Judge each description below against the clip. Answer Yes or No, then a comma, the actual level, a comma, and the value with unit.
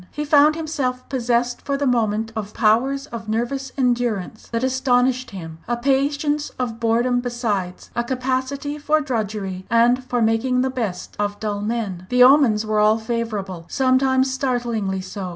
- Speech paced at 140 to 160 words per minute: Yes, average, 155 wpm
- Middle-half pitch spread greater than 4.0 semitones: No, average, 3.3 semitones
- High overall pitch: Yes, high, 240 Hz